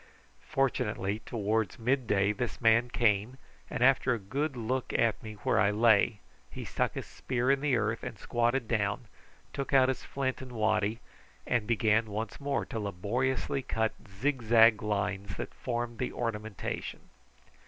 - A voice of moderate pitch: No, low, 115 Hz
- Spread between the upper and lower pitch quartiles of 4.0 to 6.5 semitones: No, average, 3.2 semitones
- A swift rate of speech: No, average, 155 wpm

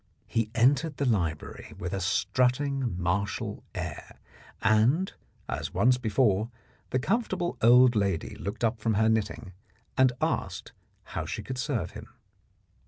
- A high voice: No, low, 115 Hz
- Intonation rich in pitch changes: No, average, 4.1 semitones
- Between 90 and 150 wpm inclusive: Yes, slow, 135 wpm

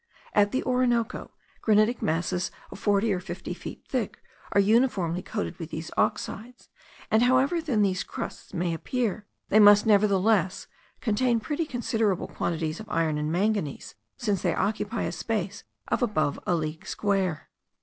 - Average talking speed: Yes, average, 150 wpm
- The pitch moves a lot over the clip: No, average, 4.2 semitones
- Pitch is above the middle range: Yes, high, 205 Hz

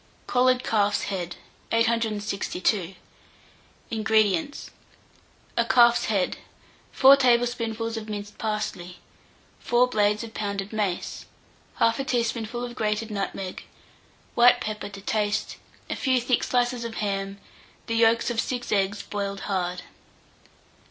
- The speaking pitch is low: No, high, 220 Hz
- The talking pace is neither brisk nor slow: No, slow, 115 wpm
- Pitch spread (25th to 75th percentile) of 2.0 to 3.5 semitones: Yes, average, 2.8 semitones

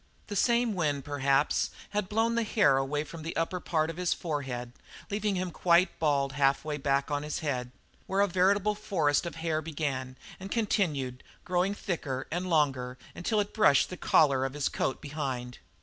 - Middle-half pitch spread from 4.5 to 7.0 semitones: Yes, average, 5.3 semitones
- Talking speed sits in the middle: Yes, average, 180 wpm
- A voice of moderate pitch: Yes, medium, 155 Hz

